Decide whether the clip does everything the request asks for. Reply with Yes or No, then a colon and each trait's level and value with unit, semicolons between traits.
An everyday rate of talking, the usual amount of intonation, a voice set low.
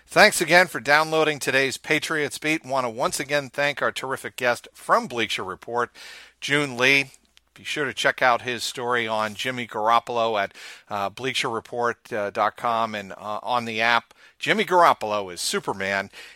Yes: average, 160 wpm; average, 4.2 semitones; low, 125 Hz